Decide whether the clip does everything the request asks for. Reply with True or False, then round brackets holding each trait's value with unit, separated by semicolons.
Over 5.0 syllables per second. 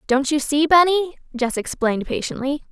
True (5.7 syllables/s)